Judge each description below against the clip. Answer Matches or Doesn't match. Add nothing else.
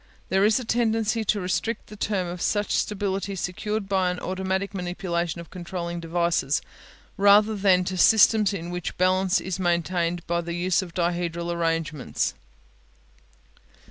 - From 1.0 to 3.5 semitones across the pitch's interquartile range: Matches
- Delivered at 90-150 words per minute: Matches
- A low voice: Doesn't match